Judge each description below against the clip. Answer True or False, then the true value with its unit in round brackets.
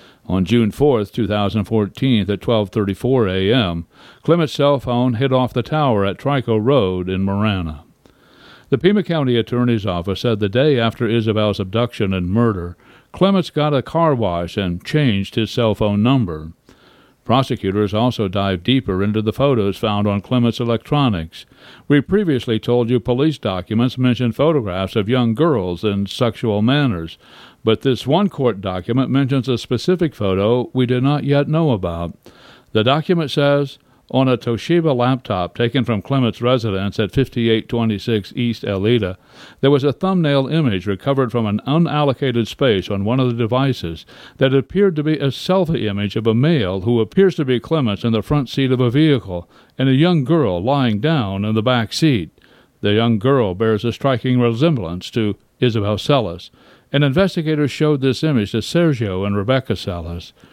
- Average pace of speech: True (165 wpm)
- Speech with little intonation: False (4.8 semitones)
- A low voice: True (120 Hz)